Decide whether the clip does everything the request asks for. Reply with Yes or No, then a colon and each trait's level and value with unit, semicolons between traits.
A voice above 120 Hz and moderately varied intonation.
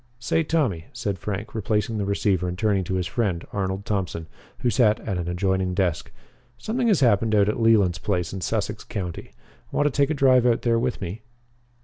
No: low, 105 Hz; average, 4.0 semitones